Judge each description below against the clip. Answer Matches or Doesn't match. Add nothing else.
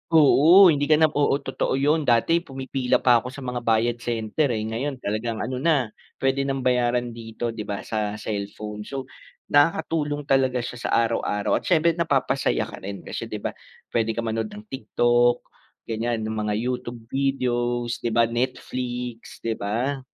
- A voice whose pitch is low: Matches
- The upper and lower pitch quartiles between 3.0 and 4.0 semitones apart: Matches